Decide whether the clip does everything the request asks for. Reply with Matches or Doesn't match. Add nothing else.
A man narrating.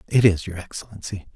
Matches